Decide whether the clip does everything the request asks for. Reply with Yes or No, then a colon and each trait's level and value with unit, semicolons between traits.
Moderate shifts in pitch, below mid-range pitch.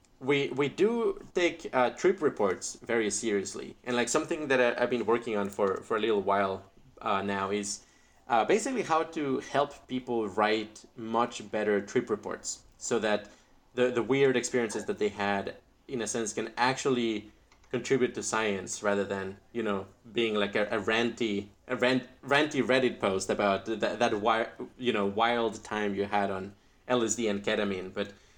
Yes: average, 3.7 semitones; low, 110 Hz